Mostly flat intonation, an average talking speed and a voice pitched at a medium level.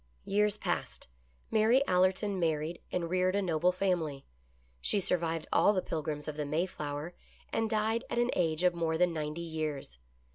No: average, 3.8 semitones; average, 170 wpm; medium, 175 Hz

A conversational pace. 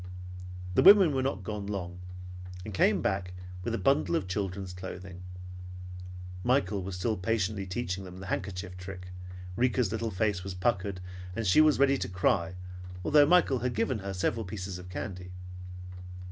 Yes: average, 160 wpm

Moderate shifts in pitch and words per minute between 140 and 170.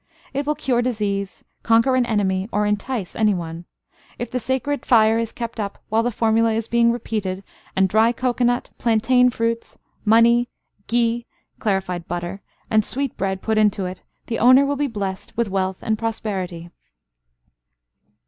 Yes: average, 3.4 semitones; average, 160 wpm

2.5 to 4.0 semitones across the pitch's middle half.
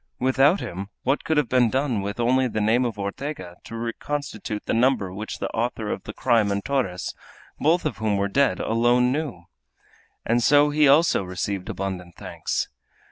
No: average, 5.2 semitones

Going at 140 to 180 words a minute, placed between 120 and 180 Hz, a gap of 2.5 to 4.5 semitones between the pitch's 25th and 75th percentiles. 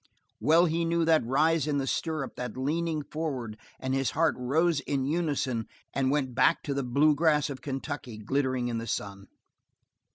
Yes: average, 175 wpm; medium, 140 Hz; average, 3.5 semitones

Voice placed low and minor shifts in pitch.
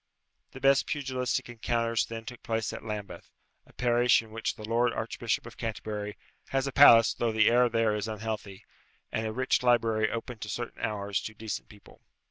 Yes: low, 115 Hz; narrow, 1.9 semitones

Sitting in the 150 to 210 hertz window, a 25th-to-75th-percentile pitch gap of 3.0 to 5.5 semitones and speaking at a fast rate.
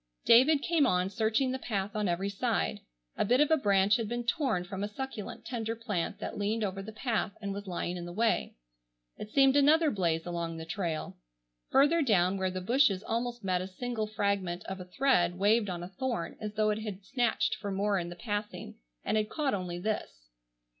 Yes: high, 205 Hz; average, 4.4 semitones; fast, 210 wpm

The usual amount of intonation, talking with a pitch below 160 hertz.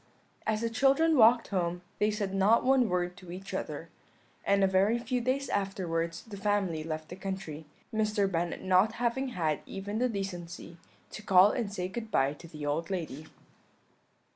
No: average, 4.1 semitones; high, 195 Hz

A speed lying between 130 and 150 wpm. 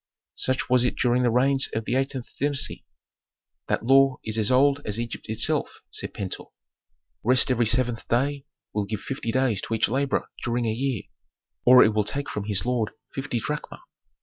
No: average, 180 wpm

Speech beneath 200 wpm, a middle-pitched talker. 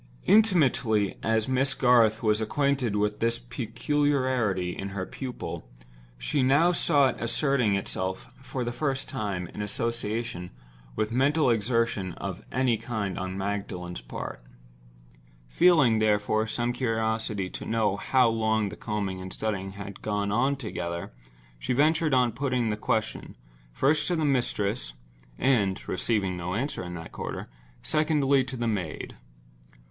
No: average, 140 wpm; low, 115 Hz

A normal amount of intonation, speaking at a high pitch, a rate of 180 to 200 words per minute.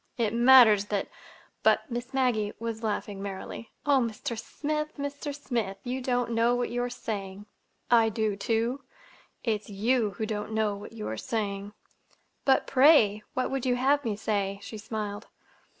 No: average, 3.3 semitones; high, 225 Hz; average, 165 wpm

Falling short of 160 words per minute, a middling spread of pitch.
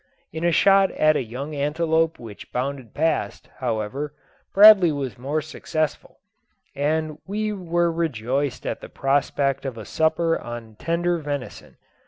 Yes: average, 140 wpm; average, 3.7 semitones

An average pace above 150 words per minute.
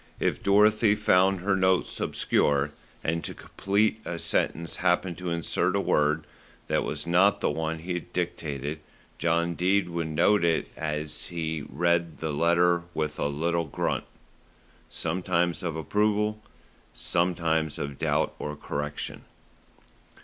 No: slow, 135 wpm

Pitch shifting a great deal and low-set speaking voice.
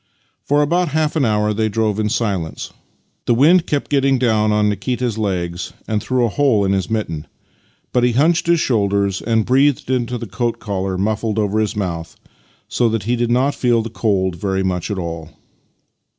No: average, 4.0 semitones; low, 110 Hz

